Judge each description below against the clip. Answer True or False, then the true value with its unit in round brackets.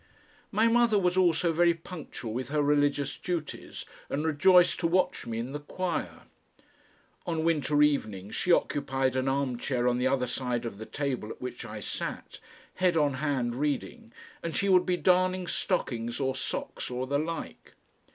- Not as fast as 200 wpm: True (170 wpm)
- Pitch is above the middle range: False (145 Hz)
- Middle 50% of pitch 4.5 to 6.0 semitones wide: True (5.4 semitones)